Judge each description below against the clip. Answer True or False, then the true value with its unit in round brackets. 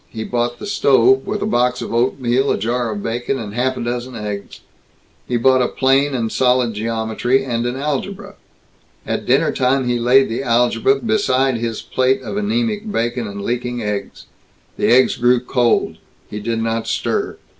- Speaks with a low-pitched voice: True (125 Hz)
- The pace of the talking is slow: False (175 wpm)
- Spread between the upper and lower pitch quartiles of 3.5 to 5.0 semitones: False (2.4 semitones)